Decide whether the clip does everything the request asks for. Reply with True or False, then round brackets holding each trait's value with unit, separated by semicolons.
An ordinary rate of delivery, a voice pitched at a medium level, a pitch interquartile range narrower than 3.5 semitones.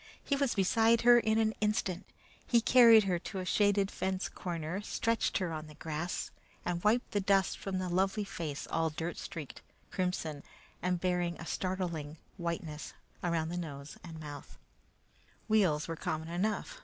False (165 wpm; 180 Hz; 4.1 semitones)